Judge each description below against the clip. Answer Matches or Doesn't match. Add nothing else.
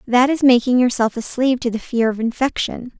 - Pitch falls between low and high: Doesn't match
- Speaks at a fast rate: Matches